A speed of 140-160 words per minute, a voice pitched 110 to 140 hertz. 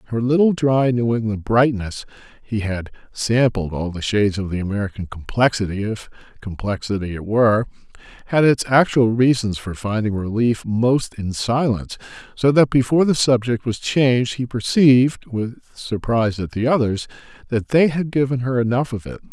Yes: average, 155 wpm; low, 115 Hz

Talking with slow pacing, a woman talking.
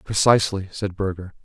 No: slow, 125 wpm; male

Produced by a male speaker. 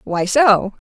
No: female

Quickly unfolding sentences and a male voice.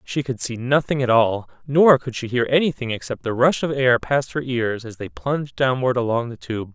Yes: fast, 230 wpm; male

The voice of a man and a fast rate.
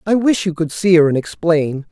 Yes: male; fast, 250 wpm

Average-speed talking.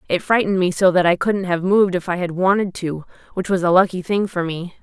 No: fast, 260 wpm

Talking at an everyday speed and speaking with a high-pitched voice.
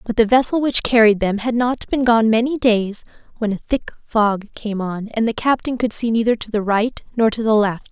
No: fast, 235 wpm; high, 225 Hz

